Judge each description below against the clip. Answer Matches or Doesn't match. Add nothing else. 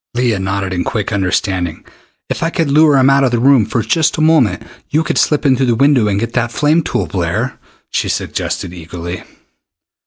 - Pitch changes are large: Matches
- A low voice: Matches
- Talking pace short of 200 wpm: Doesn't match